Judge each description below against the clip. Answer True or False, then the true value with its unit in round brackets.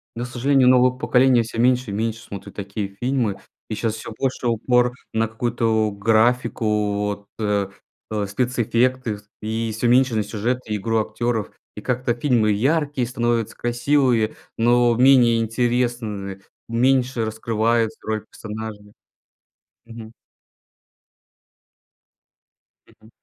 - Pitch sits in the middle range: False (115 Hz)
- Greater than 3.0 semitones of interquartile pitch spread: False (2.4 semitones)